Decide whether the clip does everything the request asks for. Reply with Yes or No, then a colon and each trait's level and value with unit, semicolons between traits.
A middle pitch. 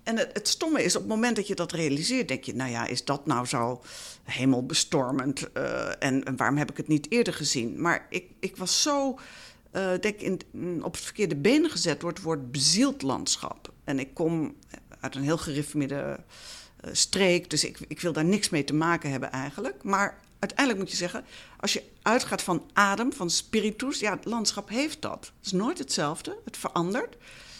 Yes: medium, 175 Hz